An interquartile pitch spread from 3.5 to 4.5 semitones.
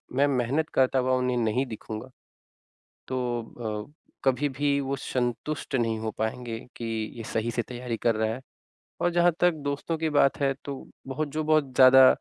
No: average, 3.1 semitones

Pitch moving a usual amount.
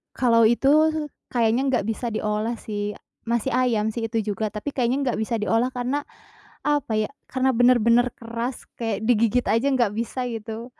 No: narrow, 2.3 semitones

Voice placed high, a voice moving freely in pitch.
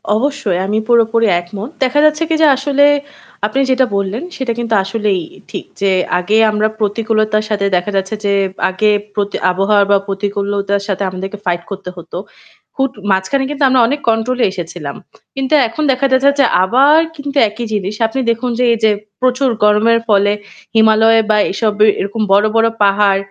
No: high, 215 Hz; average, 4.2 semitones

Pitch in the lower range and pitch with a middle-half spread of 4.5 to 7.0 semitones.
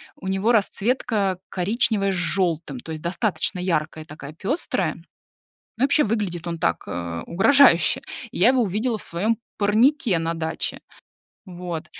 No: high, 190 Hz; average, 4.9 semitones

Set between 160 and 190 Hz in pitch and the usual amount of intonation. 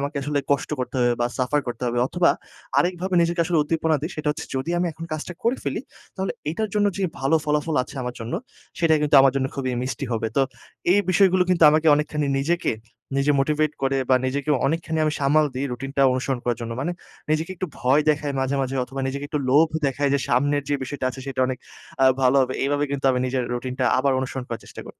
No: medium, 140 Hz; average, 3.3 semitones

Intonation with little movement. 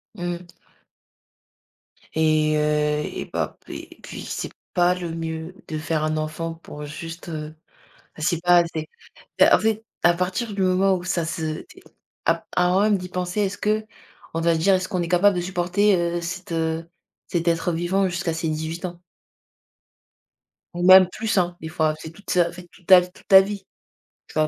Yes: narrow, 2.3 semitones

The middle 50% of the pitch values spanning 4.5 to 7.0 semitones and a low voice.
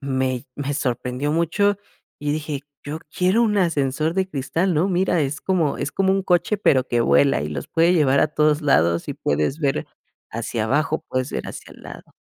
No: average, 4.8 semitones; medium, 150 Hz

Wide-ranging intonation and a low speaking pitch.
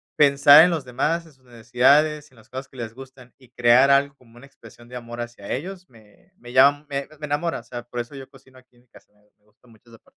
No: average, 3.0 semitones; low, 130 Hz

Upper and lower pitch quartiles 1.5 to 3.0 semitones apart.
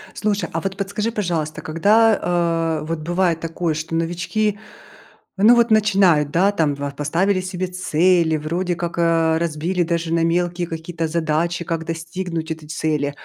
Yes: narrow, 2.4 semitones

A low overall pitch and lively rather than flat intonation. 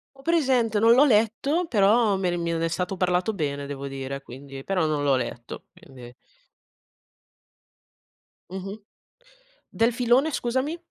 No: high, 190 Hz; wide, 8.8 semitones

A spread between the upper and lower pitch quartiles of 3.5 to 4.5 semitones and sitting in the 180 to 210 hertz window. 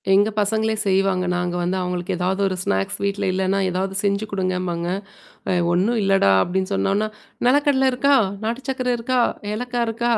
Yes: average, 4.0 semitones; high, 195 Hz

